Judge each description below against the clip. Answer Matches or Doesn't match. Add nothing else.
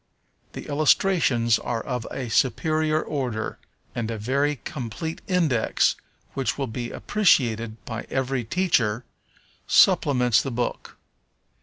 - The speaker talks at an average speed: Doesn't match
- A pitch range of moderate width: Matches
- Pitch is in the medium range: Doesn't match